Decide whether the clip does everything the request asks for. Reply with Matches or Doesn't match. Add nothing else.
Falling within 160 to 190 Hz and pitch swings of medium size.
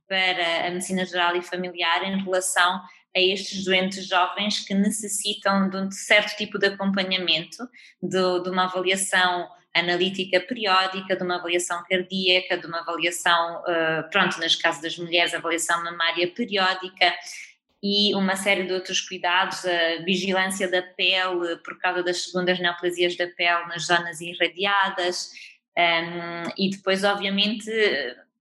Doesn't match